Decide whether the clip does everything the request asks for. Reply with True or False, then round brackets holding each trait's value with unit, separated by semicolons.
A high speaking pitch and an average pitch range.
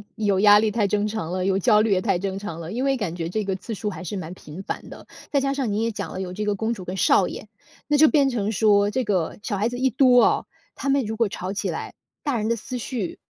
True (210 Hz; 3.6 semitones)